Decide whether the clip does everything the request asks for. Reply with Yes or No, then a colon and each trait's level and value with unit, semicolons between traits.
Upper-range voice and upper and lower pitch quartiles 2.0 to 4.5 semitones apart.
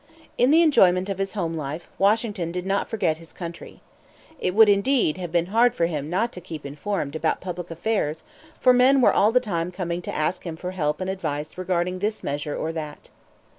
No: medium, 180 Hz; average, 4.0 semitones